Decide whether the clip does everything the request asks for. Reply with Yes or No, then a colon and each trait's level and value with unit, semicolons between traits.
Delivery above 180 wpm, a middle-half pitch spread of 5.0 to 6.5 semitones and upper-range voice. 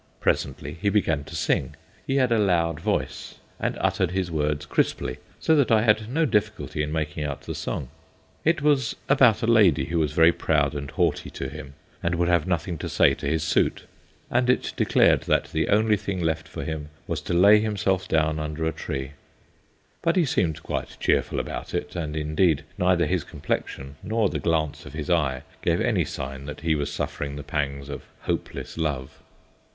No: average, 195 wpm; wide, 5.4 semitones; very low, 80 Hz